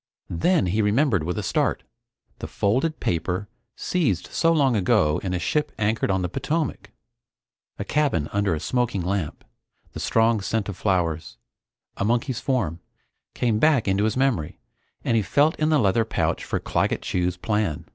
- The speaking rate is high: No, average, 165 wpm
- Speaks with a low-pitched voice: Yes, low, 105 Hz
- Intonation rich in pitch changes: Yes, wide, 6.1 semitones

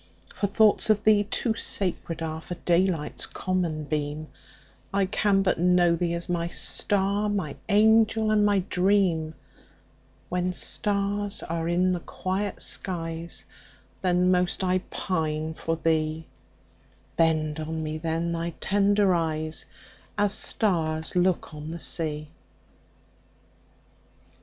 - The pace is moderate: No, slow, 105 wpm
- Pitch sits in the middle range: Yes, medium, 175 Hz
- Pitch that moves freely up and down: No, average, 3.7 semitones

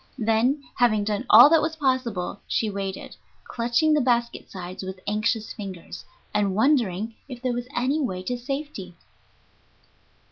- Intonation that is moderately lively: Yes, average, 4.4 semitones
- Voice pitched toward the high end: Yes, high, 230 Hz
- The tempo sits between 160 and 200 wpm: No, average, 145 wpm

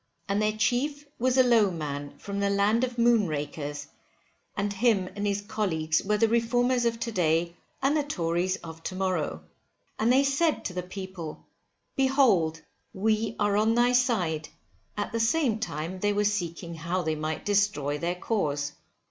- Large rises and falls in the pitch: Yes, wide, 5.7 semitones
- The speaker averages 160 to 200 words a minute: Yes, average, 170 wpm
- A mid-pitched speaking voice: No, high, 200 Hz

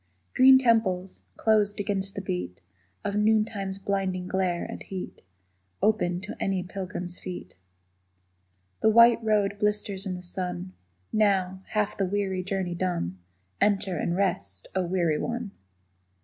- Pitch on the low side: No, high, 190 Hz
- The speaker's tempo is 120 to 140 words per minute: Yes, slow, 135 wpm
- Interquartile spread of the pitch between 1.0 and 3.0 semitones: Yes, narrow, 2.4 semitones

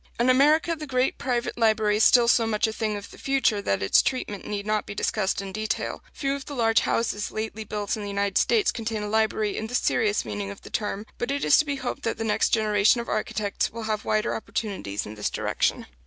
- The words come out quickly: Yes, fast, 240 wpm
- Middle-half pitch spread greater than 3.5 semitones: No, average, 2.7 semitones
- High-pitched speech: Yes, high, 220 Hz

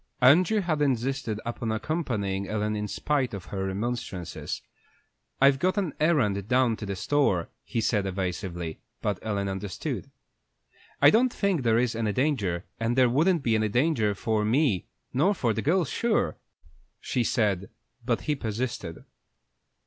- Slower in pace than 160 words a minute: Yes, average, 150 wpm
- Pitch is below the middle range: Yes, low, 115 Hz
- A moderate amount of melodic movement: No, wide, 5.9 semitones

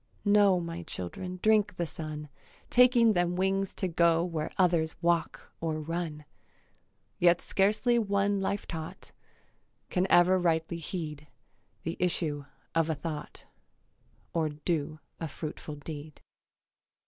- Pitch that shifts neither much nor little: Yes, average, 3.2 semitones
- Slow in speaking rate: Yes, slow, 125 wpm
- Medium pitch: Yes, medium, 170 Hz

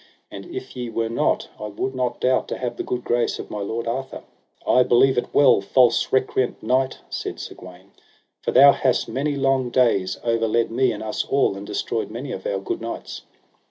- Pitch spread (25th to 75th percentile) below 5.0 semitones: Yes, average, 2.7 semitones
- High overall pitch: No, low, 120 Hz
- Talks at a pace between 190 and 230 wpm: Yes, average, 200 wpm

